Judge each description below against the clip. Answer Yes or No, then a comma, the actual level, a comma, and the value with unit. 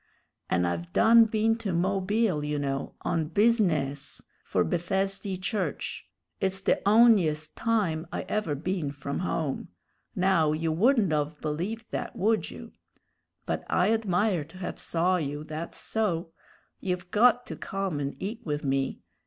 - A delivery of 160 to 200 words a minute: No, average, 145 wpm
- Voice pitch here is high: No, medium, 180 Hz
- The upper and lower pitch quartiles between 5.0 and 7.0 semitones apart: Yes, wide, 5.5 semitones